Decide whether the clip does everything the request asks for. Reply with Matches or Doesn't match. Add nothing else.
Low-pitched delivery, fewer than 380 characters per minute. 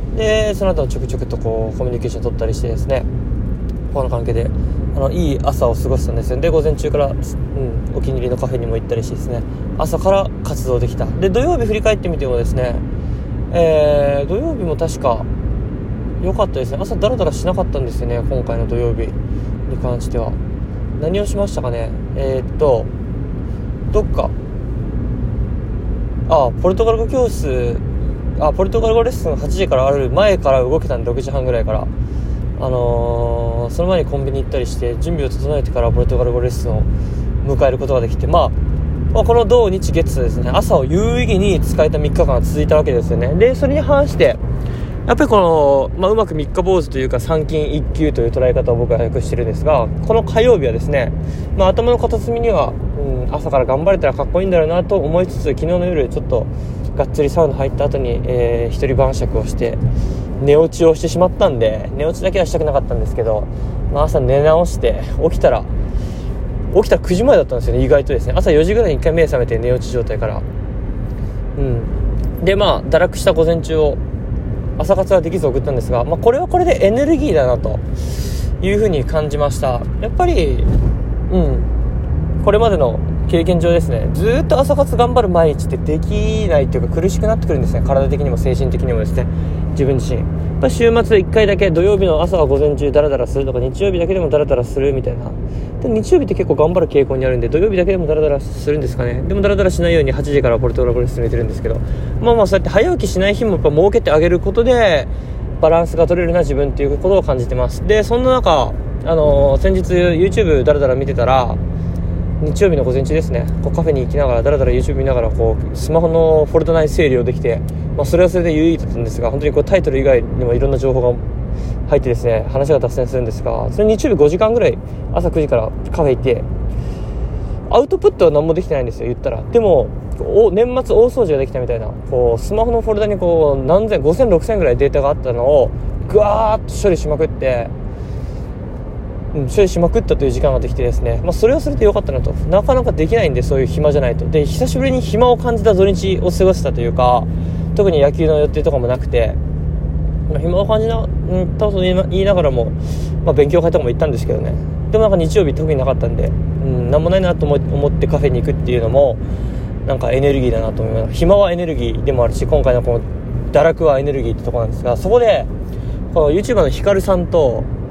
Doesn't match